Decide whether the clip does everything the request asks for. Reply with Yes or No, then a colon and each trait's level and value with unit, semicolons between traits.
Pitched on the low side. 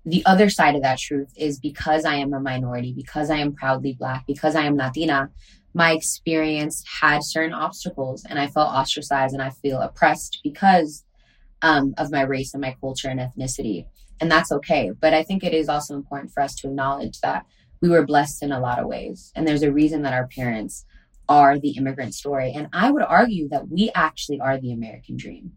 No: medium, 145 Hz